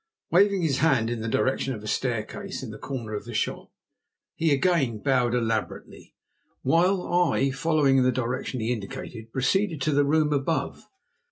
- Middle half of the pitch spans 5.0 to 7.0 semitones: Yes, average, 5.3 semitones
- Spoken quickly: No, average, 165 wpm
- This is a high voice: No, low, 135 Hz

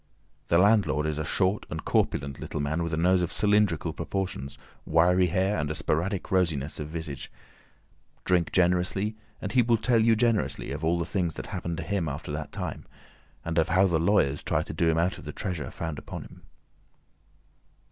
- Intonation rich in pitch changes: No, average, 3.8 semitones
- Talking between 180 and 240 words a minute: Yes, average, 195 wpm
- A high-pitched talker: No, very low, 85 Hz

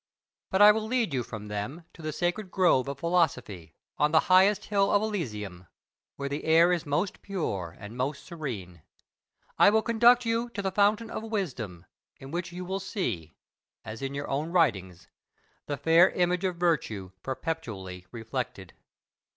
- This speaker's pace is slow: No, average, 165 wpm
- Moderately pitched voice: Yes, medium, 160 Hz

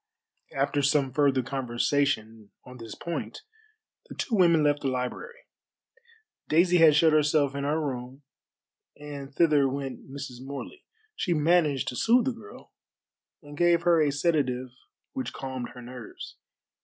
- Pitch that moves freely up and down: No, average, 3.8 semitones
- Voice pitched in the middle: Yes, medium, 145 Hz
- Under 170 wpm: Yes, average, 145 wpm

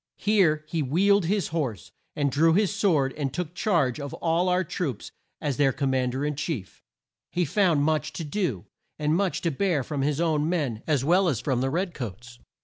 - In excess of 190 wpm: Yes, fast, 205 wpm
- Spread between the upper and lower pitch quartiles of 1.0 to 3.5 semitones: No, average, 4.6 semitones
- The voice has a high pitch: No, medium, 155 Hz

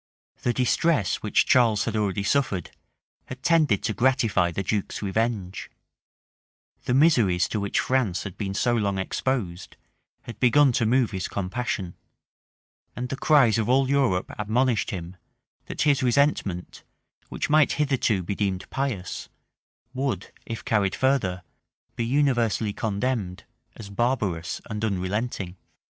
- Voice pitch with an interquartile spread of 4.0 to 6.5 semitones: Yes, average, 5.1 semitones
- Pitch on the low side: Yes, low, 110 Hz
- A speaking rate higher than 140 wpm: No, slow, 135 wpm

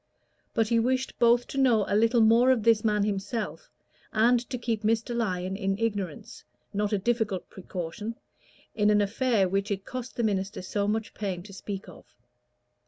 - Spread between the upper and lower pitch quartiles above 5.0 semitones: No, average, 2.8 semitones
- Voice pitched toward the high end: Yes, high, 215 Hz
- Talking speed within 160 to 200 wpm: Yes, average, 175 wpm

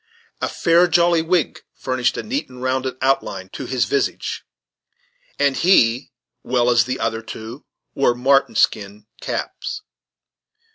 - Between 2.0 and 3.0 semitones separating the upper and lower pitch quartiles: No, average, 4.9 semitones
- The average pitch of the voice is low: Yes, low, 130 Hz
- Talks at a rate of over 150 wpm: No, slow, 135 wpm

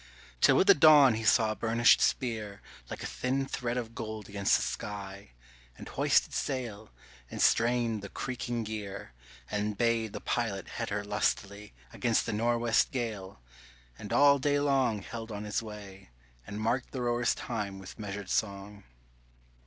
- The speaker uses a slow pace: No, average, 160 wpm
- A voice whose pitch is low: Yes, low, 110 Hz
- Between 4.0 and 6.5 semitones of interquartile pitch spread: No, average, 2.8 semitones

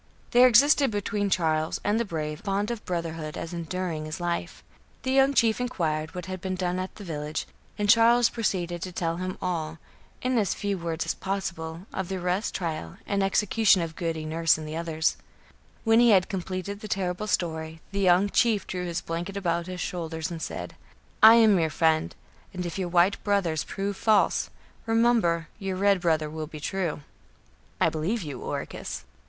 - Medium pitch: Yes, medium, 180 Hz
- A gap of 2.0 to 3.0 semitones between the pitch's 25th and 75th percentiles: No, average, 3.8 semitones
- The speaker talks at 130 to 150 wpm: No, average, 185 wpm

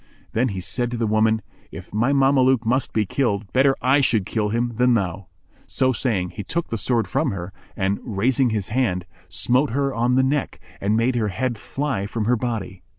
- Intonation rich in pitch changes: No, average, 3.9 semitones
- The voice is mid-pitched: No, low, 115 Hz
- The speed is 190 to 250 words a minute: Yes, fast, 205 wpm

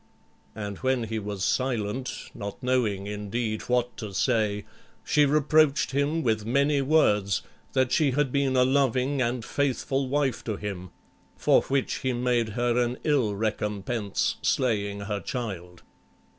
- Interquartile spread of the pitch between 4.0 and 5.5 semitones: Yes, average, 4.4 semitones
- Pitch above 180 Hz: No, low, 120 Hz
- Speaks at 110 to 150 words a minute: Yes, average, 145 wpm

